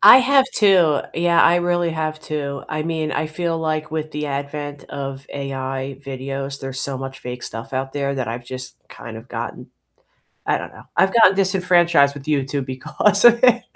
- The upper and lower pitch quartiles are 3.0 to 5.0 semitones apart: Yes, average, 4.2 semitones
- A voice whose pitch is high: No, medium, 145 Hz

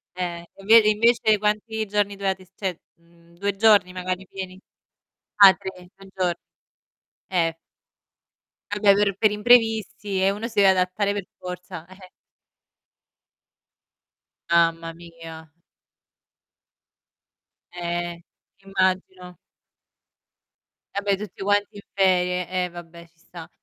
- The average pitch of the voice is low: No, high, 190 Hz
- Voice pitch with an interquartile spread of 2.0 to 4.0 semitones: Yes, narrow, 2.5 semitones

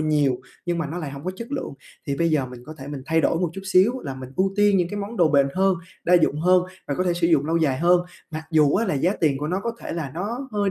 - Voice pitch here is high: No, medium, 170 Hz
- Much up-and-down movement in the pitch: No, average, 4.5 semitones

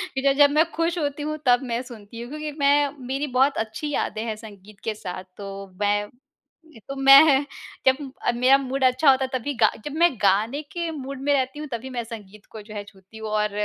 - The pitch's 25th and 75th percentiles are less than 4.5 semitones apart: No, average, 4.8 semitones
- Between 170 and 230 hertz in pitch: No, very high, 260 Hz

